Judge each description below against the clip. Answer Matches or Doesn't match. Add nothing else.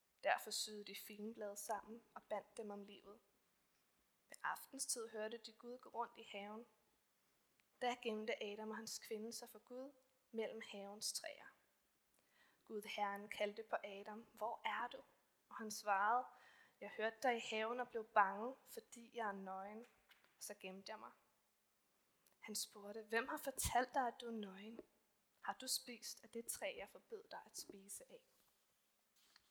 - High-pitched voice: Matches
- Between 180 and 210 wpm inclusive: Doesn't match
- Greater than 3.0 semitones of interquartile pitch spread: Doesn't match